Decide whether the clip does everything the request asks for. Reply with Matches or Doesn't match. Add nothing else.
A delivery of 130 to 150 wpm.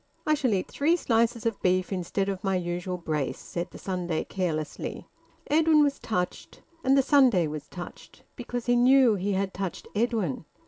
Doesn't match